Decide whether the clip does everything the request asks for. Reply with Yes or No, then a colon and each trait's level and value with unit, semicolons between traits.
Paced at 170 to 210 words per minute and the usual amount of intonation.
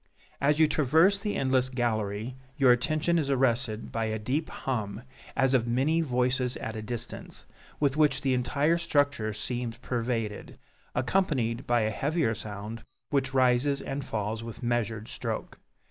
No: average, 150 wpm; average, 3.7 semitones